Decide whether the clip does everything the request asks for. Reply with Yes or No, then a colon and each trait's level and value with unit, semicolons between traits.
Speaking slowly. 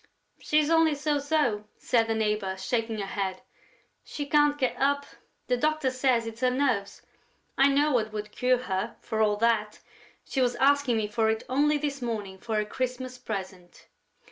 No: average, 175 wpm